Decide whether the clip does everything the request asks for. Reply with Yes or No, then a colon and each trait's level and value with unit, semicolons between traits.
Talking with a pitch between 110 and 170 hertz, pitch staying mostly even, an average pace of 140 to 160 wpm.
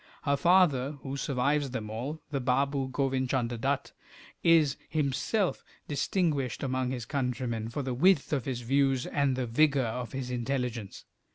Yes: low, 135 Hz; narrow, 2.3 semitones; average, 155 wpm